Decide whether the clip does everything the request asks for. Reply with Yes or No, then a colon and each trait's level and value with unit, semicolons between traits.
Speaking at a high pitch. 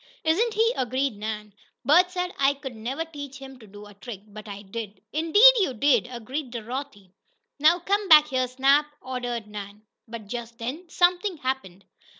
Yes: very high, 260 Hz